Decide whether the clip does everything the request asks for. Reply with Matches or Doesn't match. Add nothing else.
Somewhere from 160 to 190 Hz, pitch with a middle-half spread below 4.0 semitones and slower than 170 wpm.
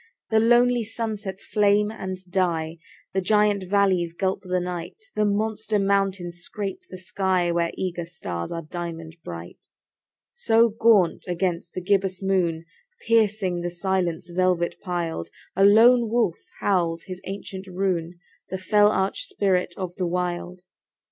Matches